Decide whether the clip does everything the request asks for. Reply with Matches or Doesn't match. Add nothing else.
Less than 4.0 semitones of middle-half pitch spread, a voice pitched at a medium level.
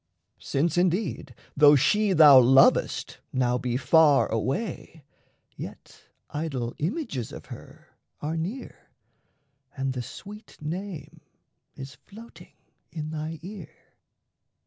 Doesn't match